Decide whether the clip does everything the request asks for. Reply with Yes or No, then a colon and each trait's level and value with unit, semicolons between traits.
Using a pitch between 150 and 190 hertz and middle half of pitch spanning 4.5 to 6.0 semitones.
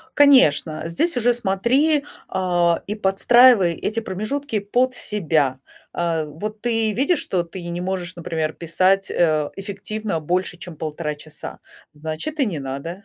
Yes: medium, 185 Hz; average, 5.2 semitones